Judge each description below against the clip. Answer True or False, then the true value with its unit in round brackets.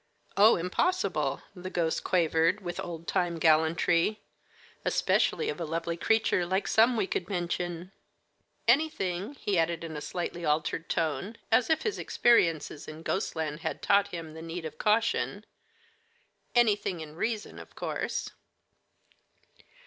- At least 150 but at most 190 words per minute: False (135 wpm)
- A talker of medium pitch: True (175 Hz)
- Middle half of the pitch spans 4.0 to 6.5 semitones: True (4.4 semitones)